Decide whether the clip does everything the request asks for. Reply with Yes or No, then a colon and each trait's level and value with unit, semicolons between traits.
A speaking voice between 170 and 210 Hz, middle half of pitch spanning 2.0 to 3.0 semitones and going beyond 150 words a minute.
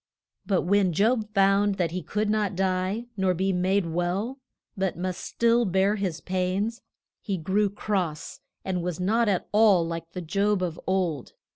Yes: high, 190 Hz; narrow, 2.5 semitones; average, 165 wpm